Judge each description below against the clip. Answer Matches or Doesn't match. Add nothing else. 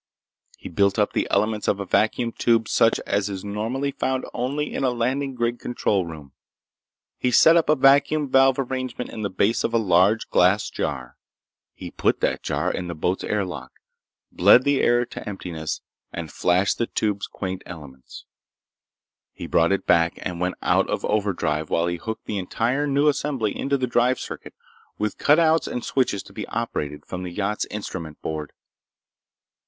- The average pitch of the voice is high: Doesn't match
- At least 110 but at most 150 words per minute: Doesn't match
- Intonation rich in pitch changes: Matches